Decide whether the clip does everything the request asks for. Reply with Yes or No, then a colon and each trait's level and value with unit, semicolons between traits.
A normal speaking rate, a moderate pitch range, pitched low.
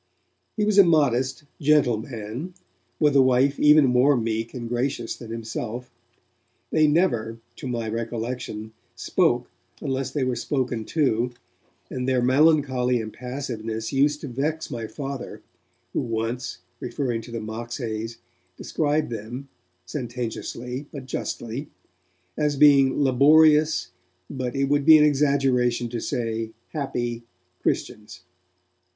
No: slow, 125 wpm; average, 3.6 semitones; low, 125 Hz